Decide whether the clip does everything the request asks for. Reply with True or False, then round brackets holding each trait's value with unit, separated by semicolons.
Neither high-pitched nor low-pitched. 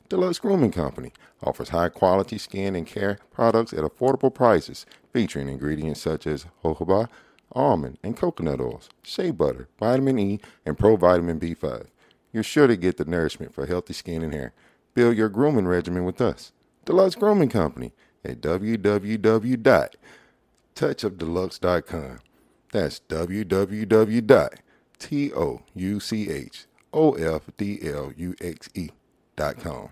False (100 Hz)